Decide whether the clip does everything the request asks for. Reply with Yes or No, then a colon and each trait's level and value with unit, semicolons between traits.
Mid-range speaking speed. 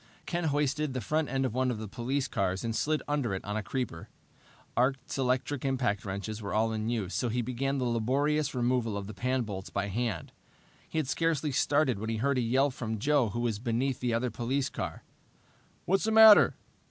No: fast, 210 wpm